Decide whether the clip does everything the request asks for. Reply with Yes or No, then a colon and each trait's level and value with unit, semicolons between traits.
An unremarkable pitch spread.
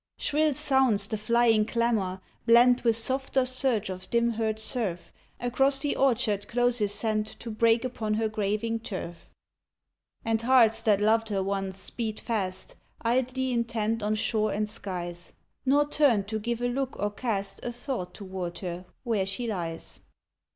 Yes: average, 3.1 semitones